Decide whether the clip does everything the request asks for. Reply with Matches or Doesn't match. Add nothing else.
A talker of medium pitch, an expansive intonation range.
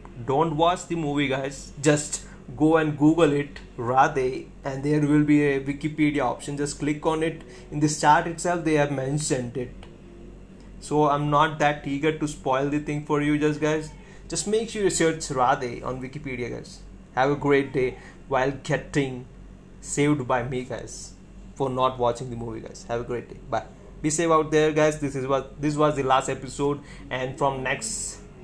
Doesn't match